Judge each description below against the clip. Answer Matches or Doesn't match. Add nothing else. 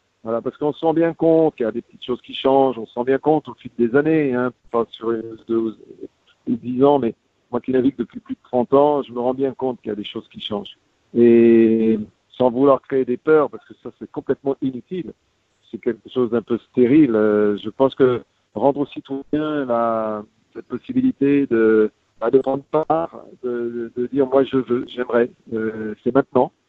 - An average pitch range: Matches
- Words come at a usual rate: Matches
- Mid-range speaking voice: Doesn't match